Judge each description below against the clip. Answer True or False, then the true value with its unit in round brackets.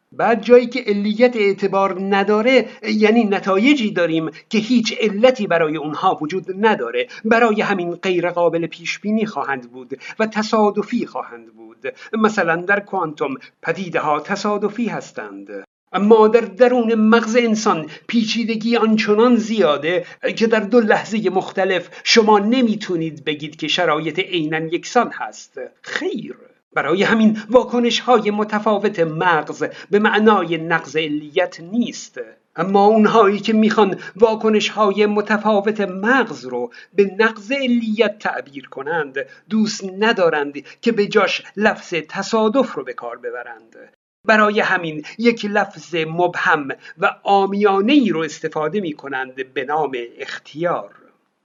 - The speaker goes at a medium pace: True (125 wpm)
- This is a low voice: False (205 Hz)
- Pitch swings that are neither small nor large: True (4.8 semitones)